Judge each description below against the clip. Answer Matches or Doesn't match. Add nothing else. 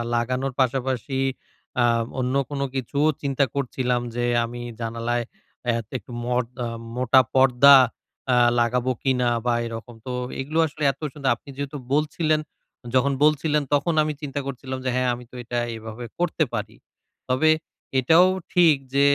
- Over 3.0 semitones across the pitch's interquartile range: Doesn't match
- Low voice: Matches